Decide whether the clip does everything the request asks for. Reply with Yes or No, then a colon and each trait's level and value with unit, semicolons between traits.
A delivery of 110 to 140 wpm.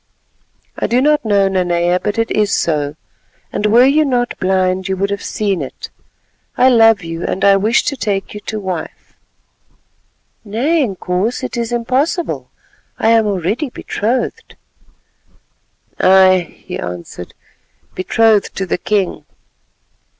Yes: slow, 135 wpm